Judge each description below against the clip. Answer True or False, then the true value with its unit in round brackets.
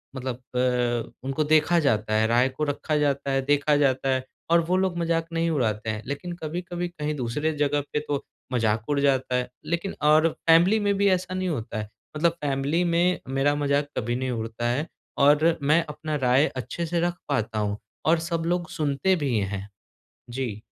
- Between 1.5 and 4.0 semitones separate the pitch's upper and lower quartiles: False (5.1 semitones)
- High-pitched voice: False (145 Hz)